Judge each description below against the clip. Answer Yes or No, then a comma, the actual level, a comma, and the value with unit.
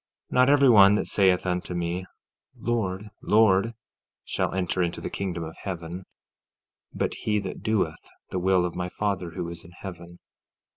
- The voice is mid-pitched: No, very low, 95 Hz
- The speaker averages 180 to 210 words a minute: No, average, 165 wpm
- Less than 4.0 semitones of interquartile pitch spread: Yes, average, 2.9 semitones